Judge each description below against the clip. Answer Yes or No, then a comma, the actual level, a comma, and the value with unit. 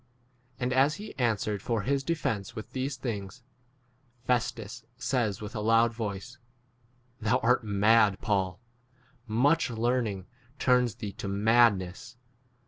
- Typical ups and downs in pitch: Yes, average, 3.4 semitones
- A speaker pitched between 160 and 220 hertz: No, low, 115 Hz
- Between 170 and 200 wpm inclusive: No, slow, 135 wpm